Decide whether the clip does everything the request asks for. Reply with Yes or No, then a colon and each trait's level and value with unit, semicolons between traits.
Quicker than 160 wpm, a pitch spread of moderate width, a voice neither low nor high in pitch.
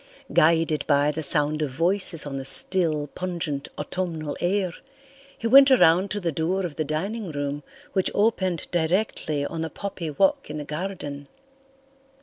No: average, 155 wpm; average, 4.0 semitones; medium, 165 Hz